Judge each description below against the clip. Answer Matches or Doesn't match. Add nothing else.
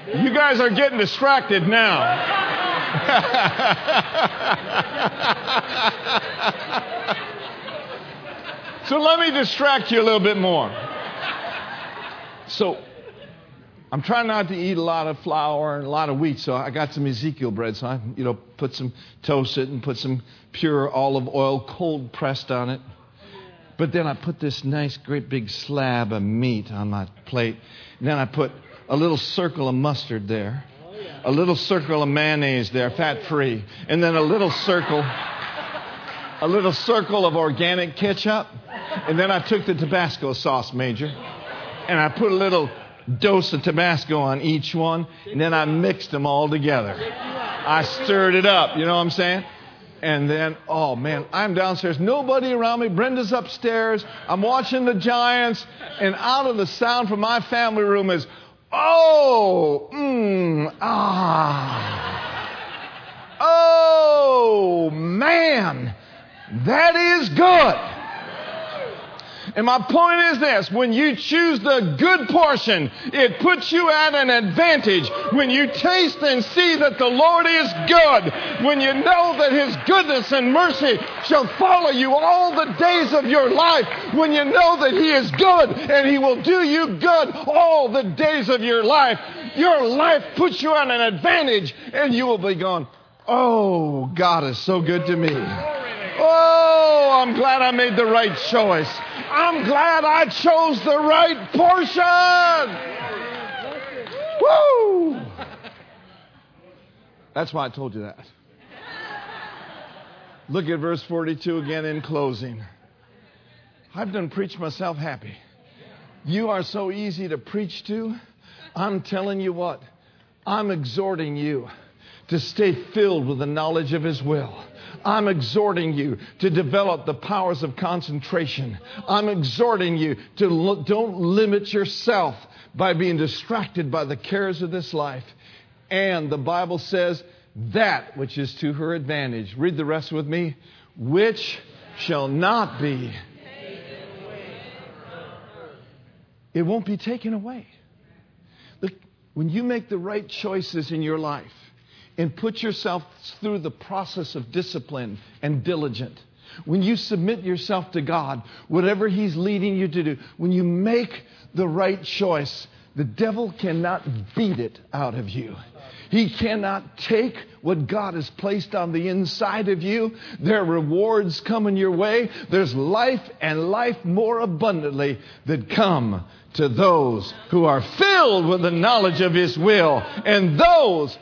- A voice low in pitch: Doesn't match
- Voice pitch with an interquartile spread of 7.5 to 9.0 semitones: Matches